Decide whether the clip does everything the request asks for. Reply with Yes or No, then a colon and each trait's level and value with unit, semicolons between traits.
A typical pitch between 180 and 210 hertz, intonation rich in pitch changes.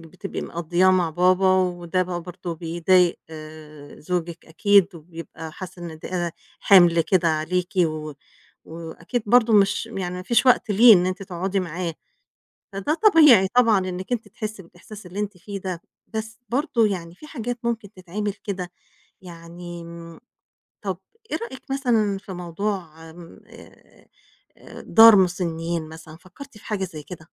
No: medium, 185 Hz; average, 3.6 semitones